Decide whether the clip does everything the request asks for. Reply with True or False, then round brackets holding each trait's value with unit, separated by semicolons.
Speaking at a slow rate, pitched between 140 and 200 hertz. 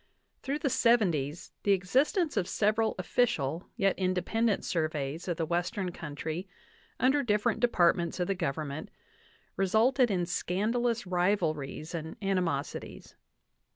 True (120 wpm; 185 Hz)